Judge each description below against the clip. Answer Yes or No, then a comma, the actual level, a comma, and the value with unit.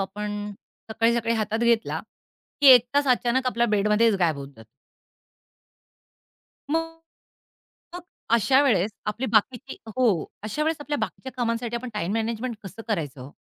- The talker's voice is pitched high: Yes, high, 230 Hz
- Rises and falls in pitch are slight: No, average, 3.2 semitones